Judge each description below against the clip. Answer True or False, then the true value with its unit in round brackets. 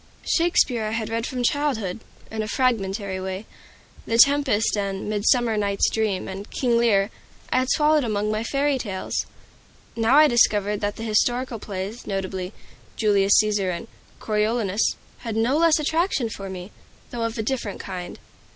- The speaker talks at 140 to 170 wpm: True (160 wpm)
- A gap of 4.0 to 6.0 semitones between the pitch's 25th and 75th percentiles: False (3.5 semitones)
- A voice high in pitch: True (220 Hz)